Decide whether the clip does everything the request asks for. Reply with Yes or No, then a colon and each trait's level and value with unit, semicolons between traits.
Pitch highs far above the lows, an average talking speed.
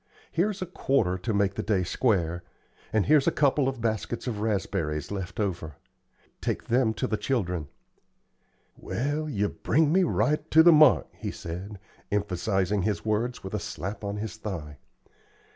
Yes: wide, 5.7 semitones; average, 160 wpm